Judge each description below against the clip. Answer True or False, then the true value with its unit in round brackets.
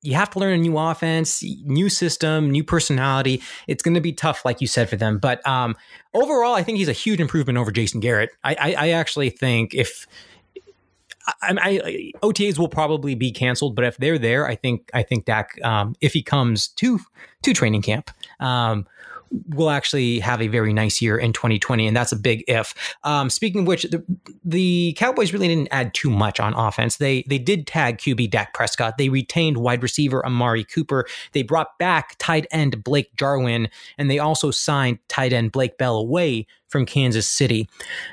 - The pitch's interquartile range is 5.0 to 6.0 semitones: True (5.4 semitones)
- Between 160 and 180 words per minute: False (195 wpm)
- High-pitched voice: False (135 Hz)